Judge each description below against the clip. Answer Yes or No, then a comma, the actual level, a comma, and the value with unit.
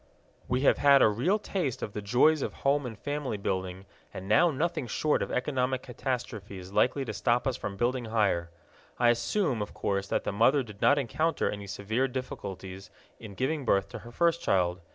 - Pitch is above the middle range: No, low, 120 Hz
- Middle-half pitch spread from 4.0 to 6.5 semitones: Yes, wide, 5.4 semitones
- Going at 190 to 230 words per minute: Yes, average, 195 wpm